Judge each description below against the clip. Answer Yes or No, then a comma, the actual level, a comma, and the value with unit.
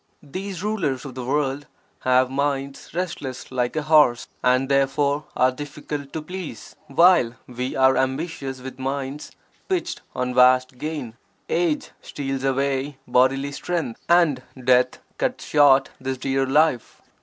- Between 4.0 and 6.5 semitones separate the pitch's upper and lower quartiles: No, narrow, 2.6 semitones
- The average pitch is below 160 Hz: Yes, low, 135 Hz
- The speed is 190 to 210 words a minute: No, slow, 135 wpm